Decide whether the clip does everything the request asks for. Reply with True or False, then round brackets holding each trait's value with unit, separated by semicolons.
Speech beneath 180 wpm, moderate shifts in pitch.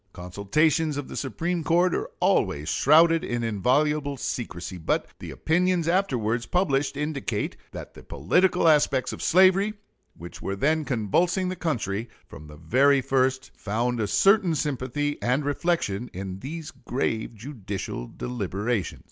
False (140 wpm; 7.1 semitones)